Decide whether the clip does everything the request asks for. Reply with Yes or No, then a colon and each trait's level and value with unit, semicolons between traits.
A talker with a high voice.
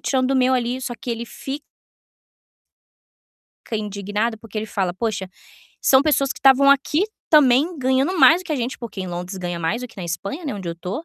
Yes: high, 240 Hz